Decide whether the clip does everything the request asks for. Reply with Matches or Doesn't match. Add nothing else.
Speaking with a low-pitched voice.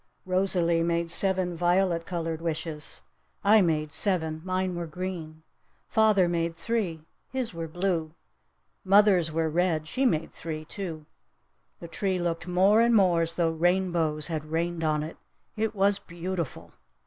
Doesn't match